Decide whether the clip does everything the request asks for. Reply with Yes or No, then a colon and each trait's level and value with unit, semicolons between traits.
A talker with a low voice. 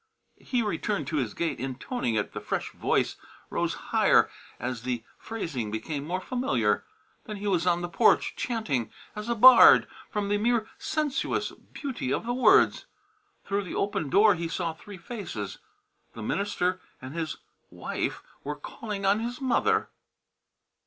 No: high, 195 Hz